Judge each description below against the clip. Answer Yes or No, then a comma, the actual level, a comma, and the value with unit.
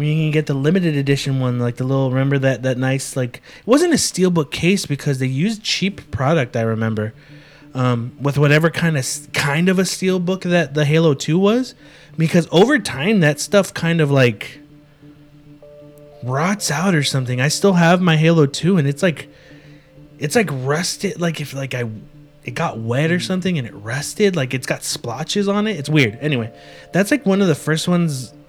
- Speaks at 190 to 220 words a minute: Yes, average, 200 wpm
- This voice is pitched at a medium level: Yes, medium, 150 Hz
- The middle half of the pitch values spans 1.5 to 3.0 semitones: No, average, 4.5 semitones